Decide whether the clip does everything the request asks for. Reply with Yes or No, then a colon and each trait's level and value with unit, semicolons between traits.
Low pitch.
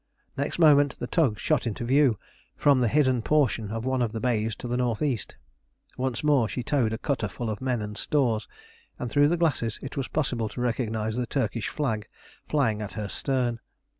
Yes: low, 125 Hz